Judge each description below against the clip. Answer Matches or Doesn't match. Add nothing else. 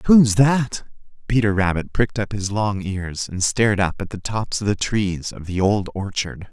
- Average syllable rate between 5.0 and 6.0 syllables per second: Doesn't match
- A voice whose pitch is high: Doesn't match